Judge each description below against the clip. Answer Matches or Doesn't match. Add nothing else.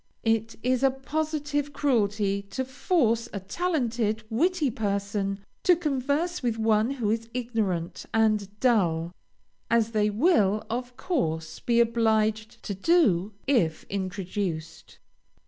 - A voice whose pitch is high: Matches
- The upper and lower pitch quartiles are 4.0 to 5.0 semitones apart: Matches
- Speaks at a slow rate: Matches